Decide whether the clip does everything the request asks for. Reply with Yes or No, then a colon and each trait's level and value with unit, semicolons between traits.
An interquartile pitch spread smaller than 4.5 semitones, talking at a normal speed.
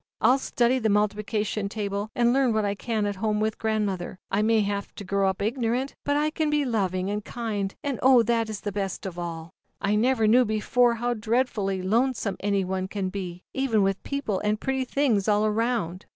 No: average, 3.3 semitones; fast, 235 wpm